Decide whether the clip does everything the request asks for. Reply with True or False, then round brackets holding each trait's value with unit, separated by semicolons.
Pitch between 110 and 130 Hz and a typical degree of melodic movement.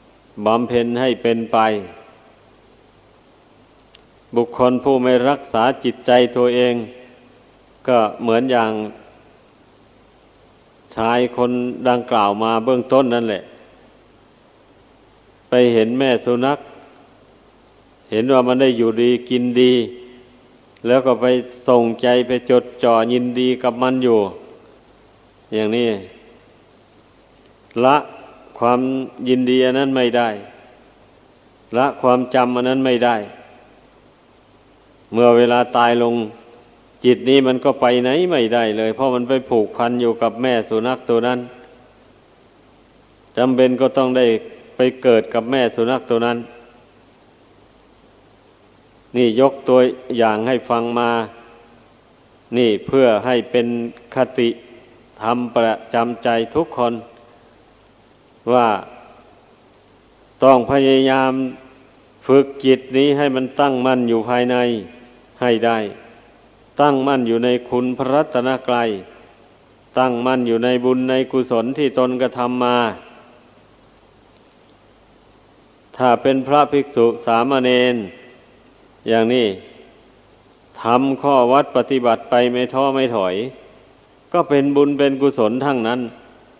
False (125 Hz; 1.6 semitones)